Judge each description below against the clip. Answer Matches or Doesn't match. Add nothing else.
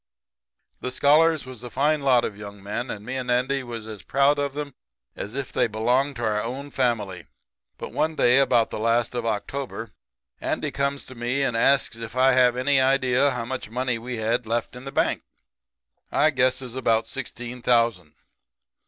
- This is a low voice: Matches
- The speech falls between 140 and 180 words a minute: Doesn't match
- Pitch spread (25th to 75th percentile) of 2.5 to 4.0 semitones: Matches